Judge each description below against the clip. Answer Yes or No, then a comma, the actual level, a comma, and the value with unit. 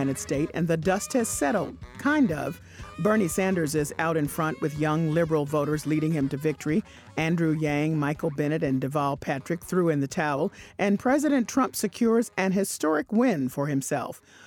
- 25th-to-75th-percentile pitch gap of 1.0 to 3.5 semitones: No, average, 4.5 semitones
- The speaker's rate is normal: Yes, average, 175 wpm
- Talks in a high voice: No, medium, 155 Hz